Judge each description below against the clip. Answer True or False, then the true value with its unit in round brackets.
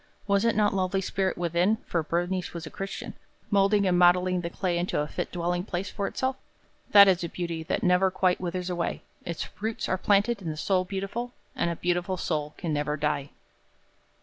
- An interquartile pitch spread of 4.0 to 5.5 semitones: False (2.4 semitones)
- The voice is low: False (180 Hz)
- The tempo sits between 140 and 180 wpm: False (200 wpm)